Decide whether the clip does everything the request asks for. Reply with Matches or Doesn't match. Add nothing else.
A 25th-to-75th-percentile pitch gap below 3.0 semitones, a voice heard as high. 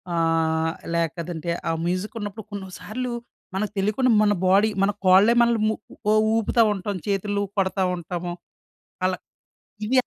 Doesn't match